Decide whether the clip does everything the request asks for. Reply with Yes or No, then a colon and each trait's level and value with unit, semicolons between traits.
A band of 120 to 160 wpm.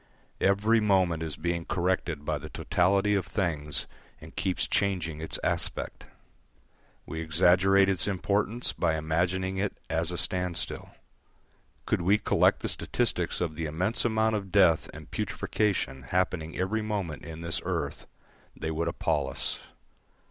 Yes: average, 145 wpm